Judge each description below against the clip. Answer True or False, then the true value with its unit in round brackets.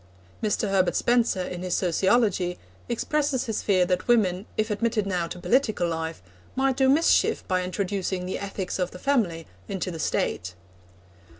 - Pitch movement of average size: True (4.4 semitones)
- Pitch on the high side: True (195 Hz)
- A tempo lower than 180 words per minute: True (160 wpm)